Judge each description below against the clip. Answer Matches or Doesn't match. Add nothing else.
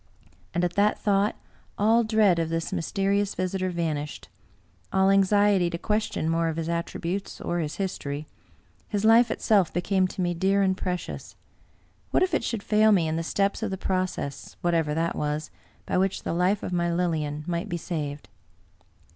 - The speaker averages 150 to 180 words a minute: Doesn't match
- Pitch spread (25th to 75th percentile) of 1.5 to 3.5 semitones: Matches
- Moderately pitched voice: Matches